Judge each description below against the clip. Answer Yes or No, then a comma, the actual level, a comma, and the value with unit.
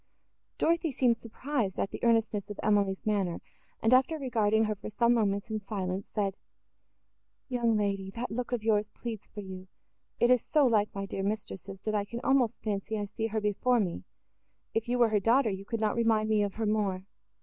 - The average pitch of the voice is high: Yes, high, 215 Hz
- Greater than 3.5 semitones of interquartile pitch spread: No, average, 2.7 semitones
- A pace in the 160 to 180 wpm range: No, average, 195 wpm